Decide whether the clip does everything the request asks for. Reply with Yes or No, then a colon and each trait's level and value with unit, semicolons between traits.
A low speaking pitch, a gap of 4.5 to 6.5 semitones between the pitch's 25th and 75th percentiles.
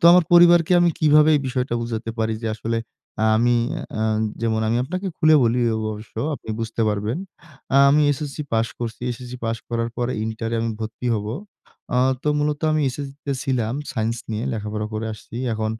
Yes: low, 120 Hz; average, 4.8 semitones